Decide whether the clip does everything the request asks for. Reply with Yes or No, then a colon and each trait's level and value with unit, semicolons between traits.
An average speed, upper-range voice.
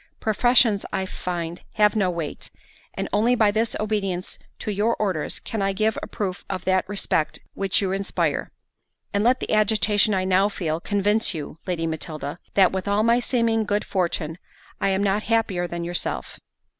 Yes: average, 170 wpm; high, 195 Hz